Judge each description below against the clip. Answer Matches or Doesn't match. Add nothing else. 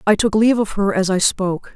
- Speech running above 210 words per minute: Matches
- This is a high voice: Matches